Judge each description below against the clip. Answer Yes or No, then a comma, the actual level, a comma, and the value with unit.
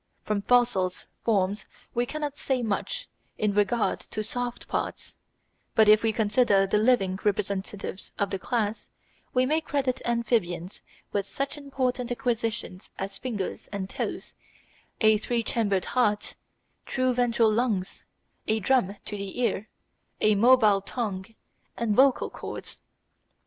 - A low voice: No, high, 220 Hz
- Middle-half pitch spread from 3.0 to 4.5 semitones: Yes, average, 3.6 semitones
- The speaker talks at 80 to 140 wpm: Yes, slow, 135 wpm